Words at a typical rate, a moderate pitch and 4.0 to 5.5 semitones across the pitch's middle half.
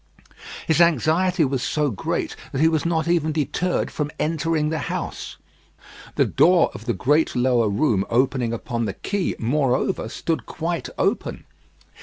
Yes: average, 150 wpm; medium, 150 Hz; average, 4.8 semitones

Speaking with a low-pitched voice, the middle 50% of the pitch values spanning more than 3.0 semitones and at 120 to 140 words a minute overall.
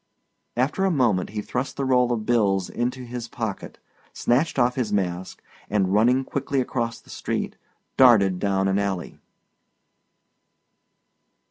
Yes: low, 120 Hz; average, 4.3 semitones; slow, 135 wpm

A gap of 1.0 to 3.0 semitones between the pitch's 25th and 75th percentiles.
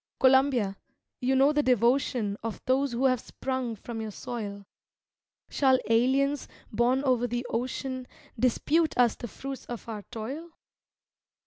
Yes: average, 2.7 semitones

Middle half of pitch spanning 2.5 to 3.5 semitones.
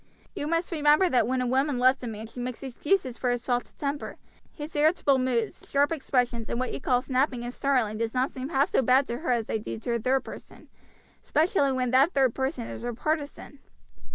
Yes: average, 2.8 semitones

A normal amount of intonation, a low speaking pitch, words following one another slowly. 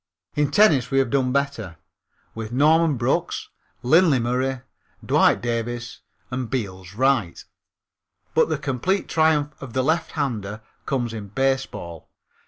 Yes: average, 3.8 semitones; low, 130 Hz; slow, 125 wpm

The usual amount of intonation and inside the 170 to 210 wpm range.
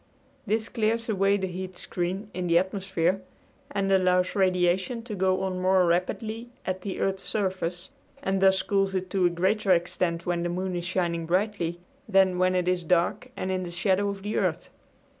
No: narrow, 1.7 semitones; average, 185 wpm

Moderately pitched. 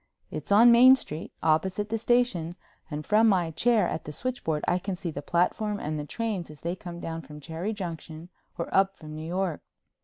Yes: medium, 175 Hz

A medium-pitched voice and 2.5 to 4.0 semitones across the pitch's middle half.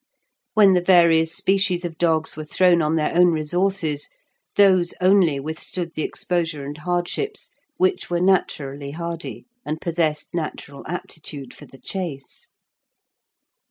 Yes: medium, 170 Hz; average, 2.8 semitones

